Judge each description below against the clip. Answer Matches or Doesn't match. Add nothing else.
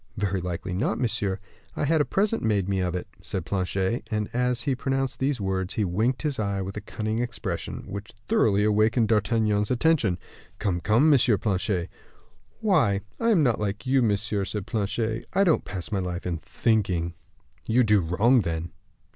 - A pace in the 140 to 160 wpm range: Doesn't match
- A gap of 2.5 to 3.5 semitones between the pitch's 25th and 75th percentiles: Doesn't match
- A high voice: Doesn't match